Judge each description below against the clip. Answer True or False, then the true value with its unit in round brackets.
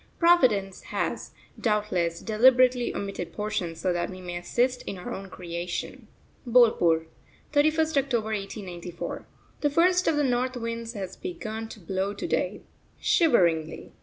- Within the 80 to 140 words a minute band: True (135 wpm)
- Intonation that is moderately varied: False (5.9 semitones)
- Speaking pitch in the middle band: False (215 Hz)